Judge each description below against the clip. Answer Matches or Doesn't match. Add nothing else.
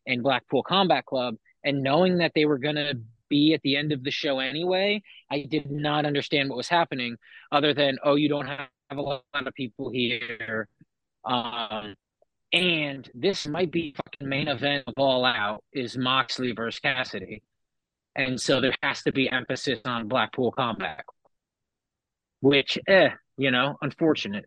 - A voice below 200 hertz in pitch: Matches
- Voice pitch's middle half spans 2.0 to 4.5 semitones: Matches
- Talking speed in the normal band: Matches